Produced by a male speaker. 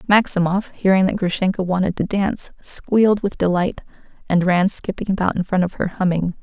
No: female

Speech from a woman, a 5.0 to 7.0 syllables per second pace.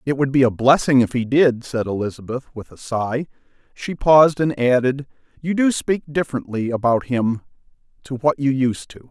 No: male; 5.1 syllables/s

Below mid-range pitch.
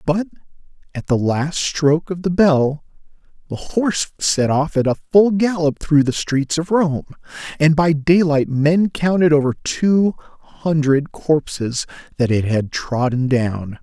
No: medium, 150 Hz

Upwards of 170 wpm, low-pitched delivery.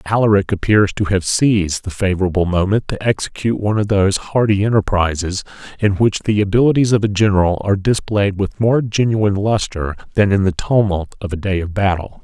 Yes: average, 180 wpm; low, 100 Hz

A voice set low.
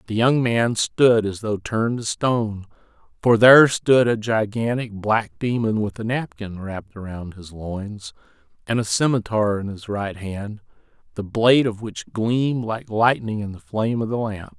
Yes: low, 110 Hz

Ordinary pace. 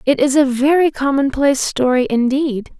Yes: average, 150 wpm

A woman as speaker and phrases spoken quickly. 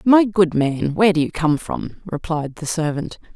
No: female; average, 195 wpm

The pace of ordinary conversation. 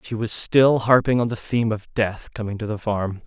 No: fast, 240 wpm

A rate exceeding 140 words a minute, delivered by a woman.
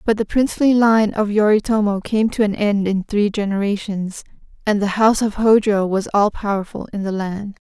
Yes: average, 190 wpm; female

